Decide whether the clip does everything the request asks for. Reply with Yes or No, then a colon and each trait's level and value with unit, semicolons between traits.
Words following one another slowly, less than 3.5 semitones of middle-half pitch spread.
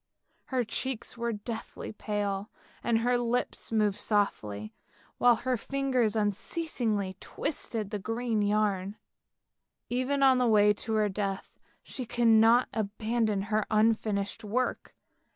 Yes: slow, 125 wpm; average, 2.7 semitones